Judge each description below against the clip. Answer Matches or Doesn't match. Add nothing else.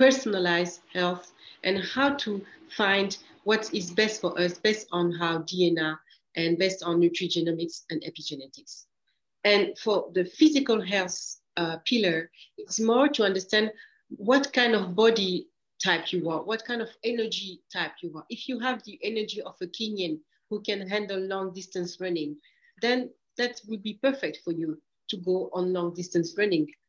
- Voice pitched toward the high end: Matches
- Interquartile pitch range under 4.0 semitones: Doesn't match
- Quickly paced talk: Doesn't match